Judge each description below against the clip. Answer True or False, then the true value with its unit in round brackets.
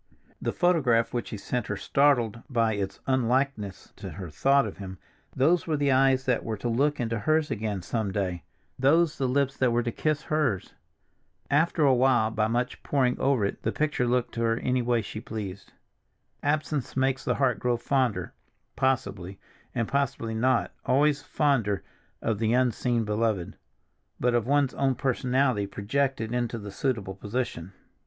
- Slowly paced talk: False (165 wpm)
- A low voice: True (125 Hz)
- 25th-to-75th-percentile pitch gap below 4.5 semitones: True (3.8 semitones)